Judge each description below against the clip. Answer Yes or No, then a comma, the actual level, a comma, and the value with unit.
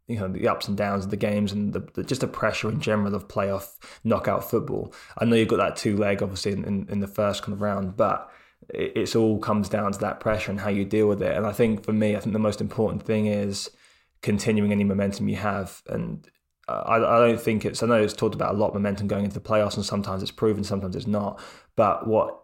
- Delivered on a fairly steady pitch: Yes, narrow, 1.2 semitones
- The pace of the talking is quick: Yes, fast, 255 wpm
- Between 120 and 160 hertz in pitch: No, low, 105 Hz